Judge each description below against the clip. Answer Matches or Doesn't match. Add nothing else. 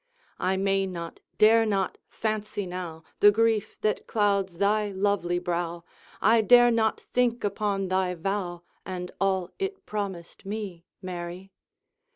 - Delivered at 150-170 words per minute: Doesn't match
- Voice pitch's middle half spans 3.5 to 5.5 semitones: Doesn't match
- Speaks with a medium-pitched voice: Doesn't match